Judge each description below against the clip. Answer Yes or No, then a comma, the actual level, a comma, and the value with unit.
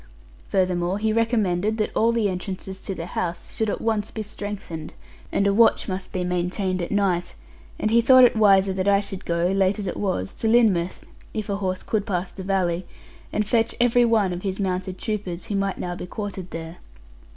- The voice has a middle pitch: No, high, 195 Hz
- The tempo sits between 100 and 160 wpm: No, fast, 205 wpm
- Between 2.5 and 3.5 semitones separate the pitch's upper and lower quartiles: Yes, average, 2.8 semitones